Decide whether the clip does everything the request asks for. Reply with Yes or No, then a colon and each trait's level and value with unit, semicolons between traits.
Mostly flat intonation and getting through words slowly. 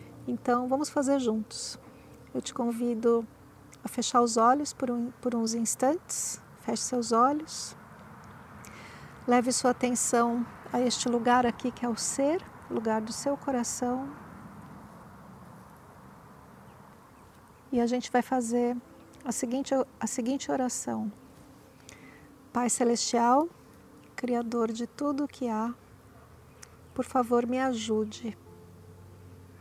Yes: narrow, 1.6 semitones; slow, 115 wpm